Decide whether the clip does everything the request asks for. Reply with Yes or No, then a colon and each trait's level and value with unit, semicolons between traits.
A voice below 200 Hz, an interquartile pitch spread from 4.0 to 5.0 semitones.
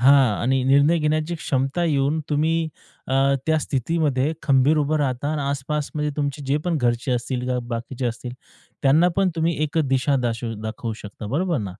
No: medium, 140 Hz; average, 3.5 semitones